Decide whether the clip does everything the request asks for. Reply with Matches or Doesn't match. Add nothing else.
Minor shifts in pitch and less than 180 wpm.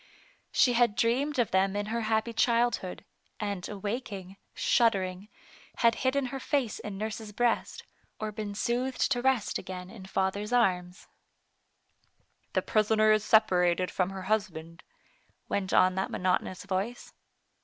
Doesn't match